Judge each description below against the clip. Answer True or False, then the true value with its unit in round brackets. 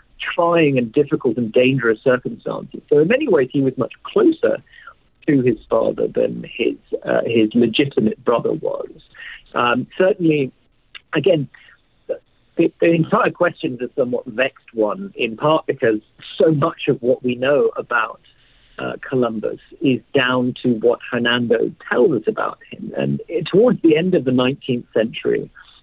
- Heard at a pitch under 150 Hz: True (140 Hz)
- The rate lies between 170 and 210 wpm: False (155 wpm)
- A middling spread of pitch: False (6.6 semitones)